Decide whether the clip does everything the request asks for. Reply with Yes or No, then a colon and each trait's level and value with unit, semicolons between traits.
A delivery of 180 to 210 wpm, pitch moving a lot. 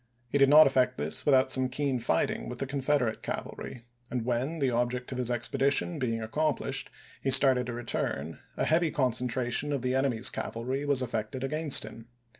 No: average, 190 wpm; narrow, 2.5 semitones